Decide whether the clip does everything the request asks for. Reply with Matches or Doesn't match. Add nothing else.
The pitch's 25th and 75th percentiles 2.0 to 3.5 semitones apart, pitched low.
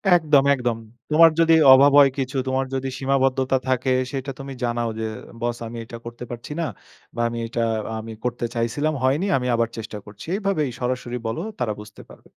Matches